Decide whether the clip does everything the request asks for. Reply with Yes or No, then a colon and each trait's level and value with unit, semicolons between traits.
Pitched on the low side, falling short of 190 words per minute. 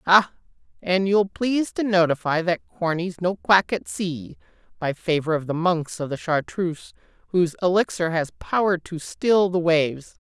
No: medium, 175 Hz; average, 165 wpm